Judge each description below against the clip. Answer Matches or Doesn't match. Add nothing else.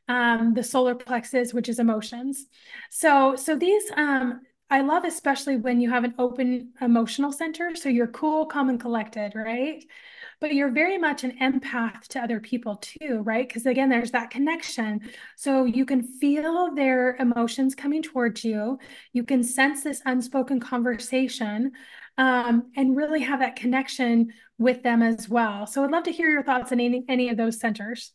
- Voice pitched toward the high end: Matches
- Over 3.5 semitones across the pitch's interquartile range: Doesn't match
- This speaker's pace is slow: Doesn't match